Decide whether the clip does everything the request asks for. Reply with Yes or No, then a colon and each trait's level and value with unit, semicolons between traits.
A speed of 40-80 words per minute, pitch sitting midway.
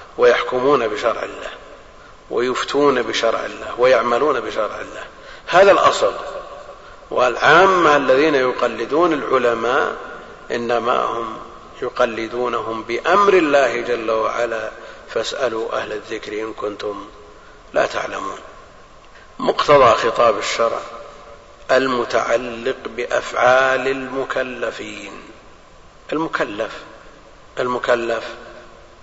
No: average, 75 wpm; low, 130 Hz